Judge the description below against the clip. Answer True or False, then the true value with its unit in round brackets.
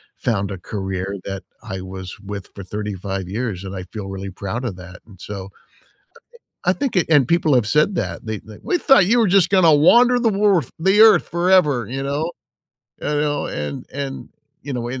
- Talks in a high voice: False (120 Hz)